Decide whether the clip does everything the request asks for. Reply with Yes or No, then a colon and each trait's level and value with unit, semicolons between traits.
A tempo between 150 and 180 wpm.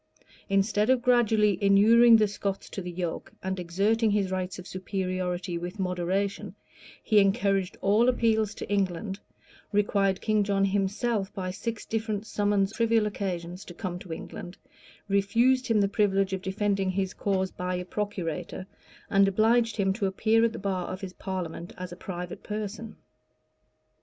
Yes: average, 160 wpm